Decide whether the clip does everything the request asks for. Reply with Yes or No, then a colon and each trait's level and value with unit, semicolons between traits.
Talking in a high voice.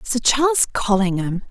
Yes: high, 220 Hz